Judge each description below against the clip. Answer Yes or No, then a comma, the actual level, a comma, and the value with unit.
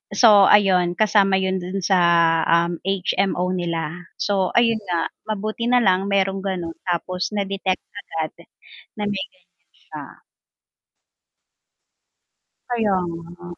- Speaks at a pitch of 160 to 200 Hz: Yes, high, 190 Hz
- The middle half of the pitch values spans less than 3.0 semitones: Yes, narrow, 2.6 semitones